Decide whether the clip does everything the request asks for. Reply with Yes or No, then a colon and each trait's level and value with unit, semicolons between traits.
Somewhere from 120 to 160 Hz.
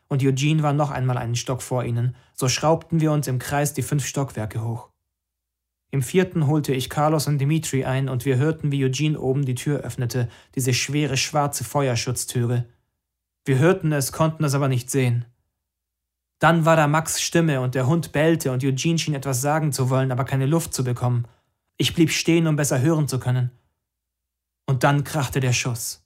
Yes: low, 135 Hz